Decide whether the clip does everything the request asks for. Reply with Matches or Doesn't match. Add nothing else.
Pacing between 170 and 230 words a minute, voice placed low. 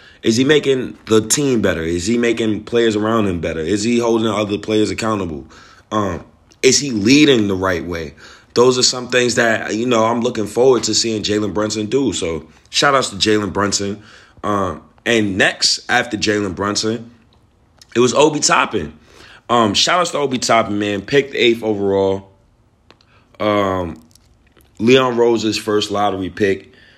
Doesn't match